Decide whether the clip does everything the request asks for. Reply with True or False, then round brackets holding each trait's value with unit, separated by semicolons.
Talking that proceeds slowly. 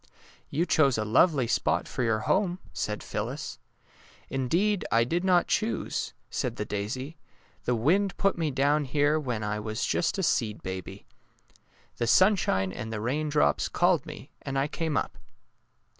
False (175 wpm)